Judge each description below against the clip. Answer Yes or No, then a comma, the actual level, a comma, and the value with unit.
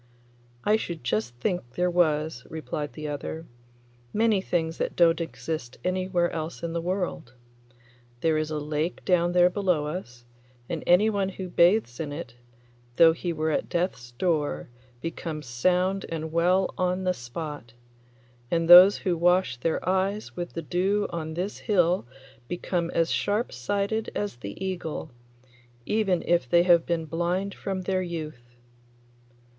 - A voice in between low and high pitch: Yes, medium, 170 Hz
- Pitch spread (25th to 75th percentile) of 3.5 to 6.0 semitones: No, average, 3.0 semitones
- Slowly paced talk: No, average, 150 wpm